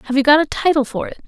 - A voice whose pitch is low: No, very high, 280 Hz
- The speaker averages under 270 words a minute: No, fast, 330 wpm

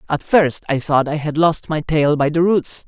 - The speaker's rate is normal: No, fast, 250 wpm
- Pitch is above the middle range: No, medium, 155 Hz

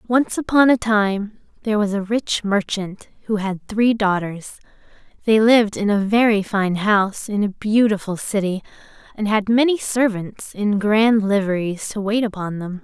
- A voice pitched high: Yes, high, 210 Hz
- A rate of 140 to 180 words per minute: Yes, average, 165 wpm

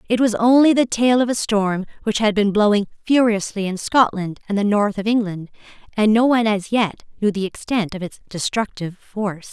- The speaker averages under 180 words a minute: No, average, 200 wpm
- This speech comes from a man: No, female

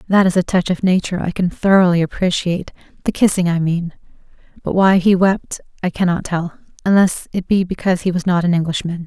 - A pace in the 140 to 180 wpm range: No, average, 190 wpm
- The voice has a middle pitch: Yes, medium, 180 Hz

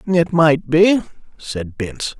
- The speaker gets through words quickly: No, slow, 135 wpm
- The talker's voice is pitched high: No, medium, 160 Hz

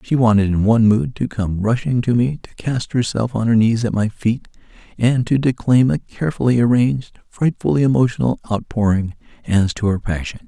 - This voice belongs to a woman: No, male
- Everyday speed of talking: Yes, average, 185 wpm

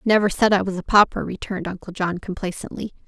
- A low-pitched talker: No, high, 190 Hz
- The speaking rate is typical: No, fast, 215 wpm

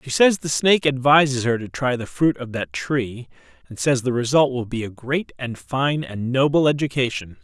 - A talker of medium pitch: No, low, 130 Hz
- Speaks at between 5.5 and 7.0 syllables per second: No, 5.0 syllables/s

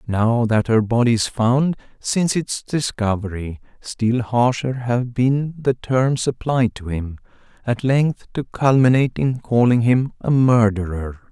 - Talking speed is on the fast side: No, average, 145 wpm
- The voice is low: Yes, low, 120 Hz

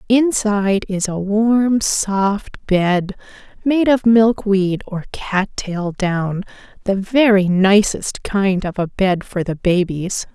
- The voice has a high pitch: Yes, high, 200 Hz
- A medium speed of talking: No, slow, 130 wpm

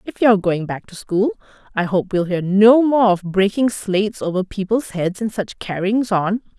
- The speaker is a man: No, female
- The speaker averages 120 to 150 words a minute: No, average, 200 wpm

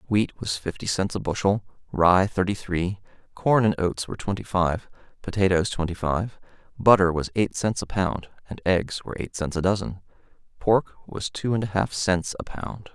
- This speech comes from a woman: No, male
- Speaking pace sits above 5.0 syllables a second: No, 4.9 syllables/s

